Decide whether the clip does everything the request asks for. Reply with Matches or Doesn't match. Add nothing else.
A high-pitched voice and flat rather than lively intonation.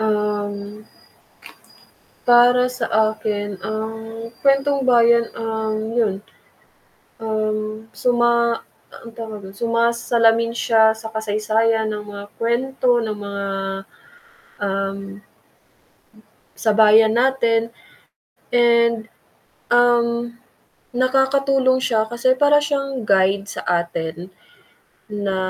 Matches